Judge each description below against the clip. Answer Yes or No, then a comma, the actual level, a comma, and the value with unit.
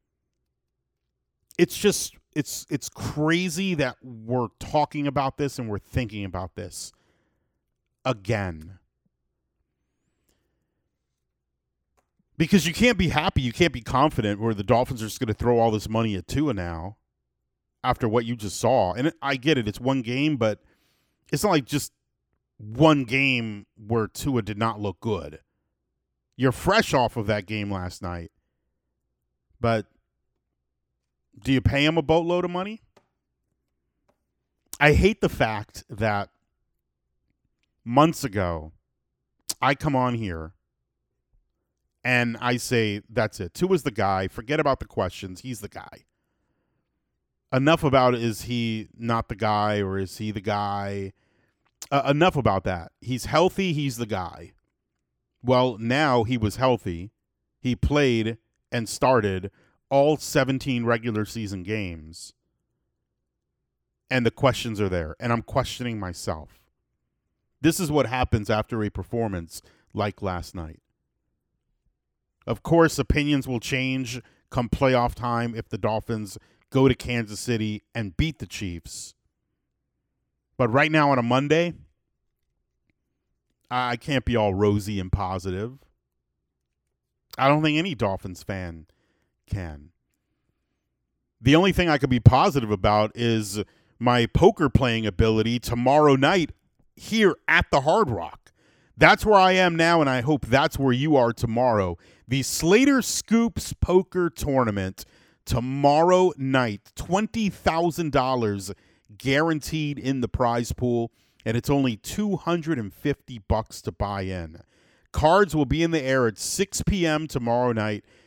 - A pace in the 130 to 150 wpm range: Yes, slow, 135 wpm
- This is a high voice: No, low, 120 Hz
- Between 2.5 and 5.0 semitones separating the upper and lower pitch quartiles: No, wide, 5.6 semitones